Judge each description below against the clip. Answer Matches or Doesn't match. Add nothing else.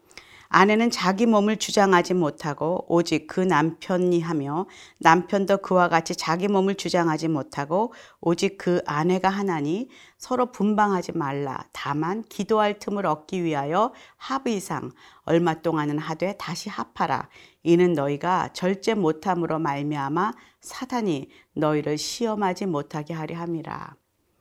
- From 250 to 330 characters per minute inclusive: Matches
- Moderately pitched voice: Matches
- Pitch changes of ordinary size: Matches